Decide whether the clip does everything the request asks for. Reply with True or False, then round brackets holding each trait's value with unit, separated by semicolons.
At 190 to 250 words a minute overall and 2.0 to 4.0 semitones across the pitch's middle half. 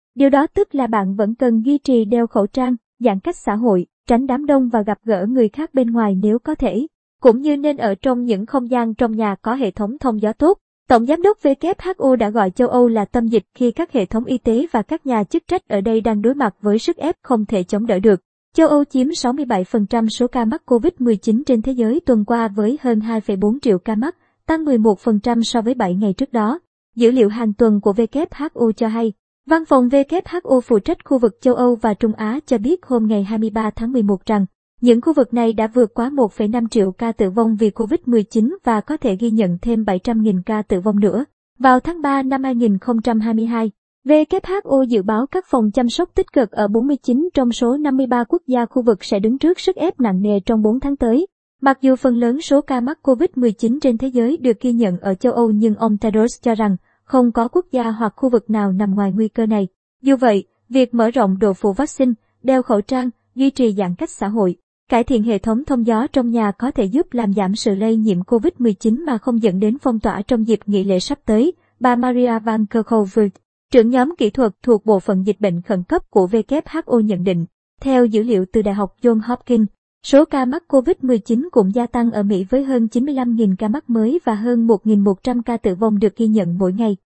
True (225 wpm; 3.3 semitones)